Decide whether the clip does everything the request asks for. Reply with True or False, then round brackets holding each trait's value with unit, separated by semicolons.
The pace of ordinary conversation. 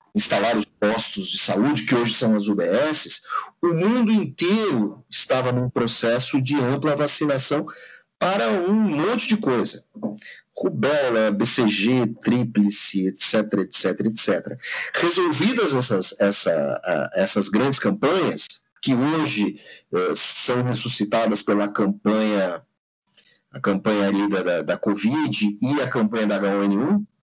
False (115 wpm)